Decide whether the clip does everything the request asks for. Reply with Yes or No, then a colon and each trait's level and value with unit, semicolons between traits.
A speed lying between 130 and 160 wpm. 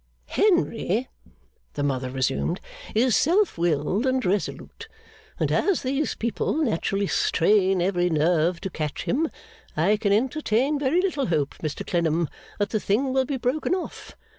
Yes: average, 145 wpm